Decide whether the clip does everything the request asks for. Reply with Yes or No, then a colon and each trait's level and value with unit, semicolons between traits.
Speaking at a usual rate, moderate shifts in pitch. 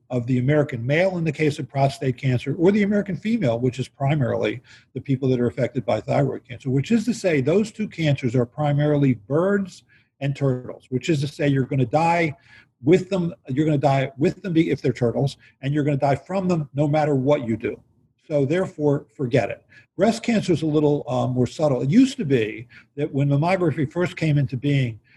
No: fast, 215 wpm; average, 4.2 semitones